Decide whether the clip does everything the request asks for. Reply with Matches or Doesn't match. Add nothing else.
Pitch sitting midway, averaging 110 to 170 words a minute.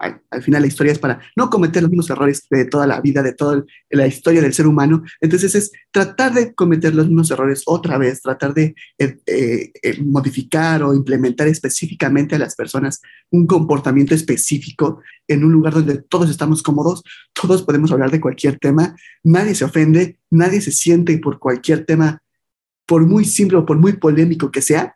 Doesn't match